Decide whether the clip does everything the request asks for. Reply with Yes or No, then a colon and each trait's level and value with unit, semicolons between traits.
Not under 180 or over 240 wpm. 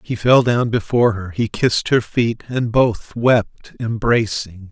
No: average, 165 wpm